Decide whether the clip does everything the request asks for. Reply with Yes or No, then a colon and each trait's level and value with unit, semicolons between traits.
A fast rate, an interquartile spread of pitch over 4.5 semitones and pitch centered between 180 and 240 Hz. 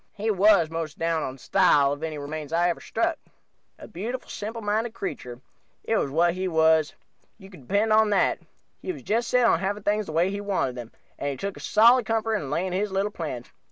Yes: fast, 220 wpm; average, 5.1 semitones; high, 190 Hz